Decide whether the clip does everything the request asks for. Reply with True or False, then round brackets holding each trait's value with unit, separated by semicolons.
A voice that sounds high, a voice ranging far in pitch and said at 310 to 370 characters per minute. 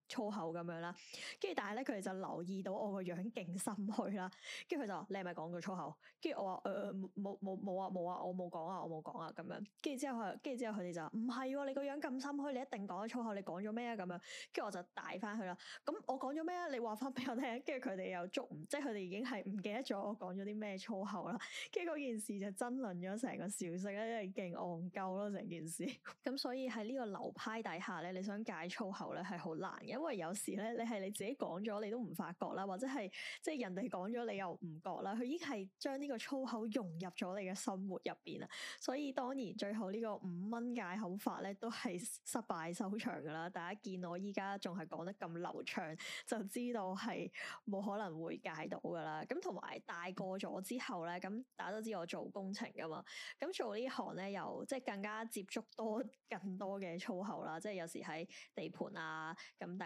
False (205 Hz; 4.7 semitones; 330 characters per minute)